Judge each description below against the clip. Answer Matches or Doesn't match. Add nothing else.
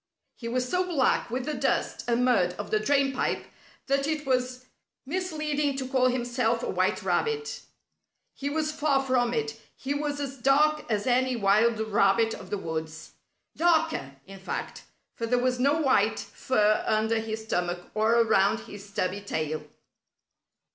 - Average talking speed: Matches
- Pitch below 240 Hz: Doesn't match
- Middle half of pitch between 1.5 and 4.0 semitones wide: Doesn't match